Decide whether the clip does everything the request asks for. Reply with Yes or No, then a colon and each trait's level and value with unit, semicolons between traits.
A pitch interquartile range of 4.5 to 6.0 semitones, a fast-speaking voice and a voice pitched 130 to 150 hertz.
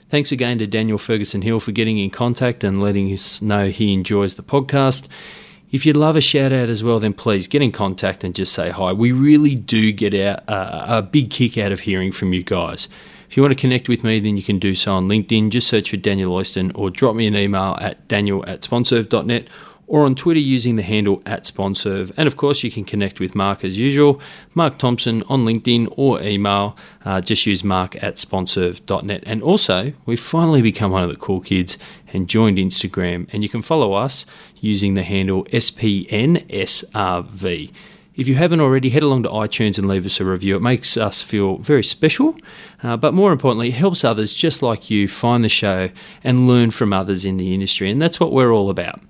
No: average, 5.1 semitones; fast, 210 wpm; low, 110 Hz